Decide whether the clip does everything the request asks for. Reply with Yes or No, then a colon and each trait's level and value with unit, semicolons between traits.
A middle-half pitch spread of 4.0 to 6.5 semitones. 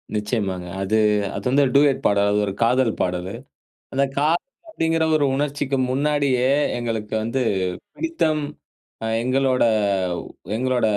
Yes: average, 5.1 semitones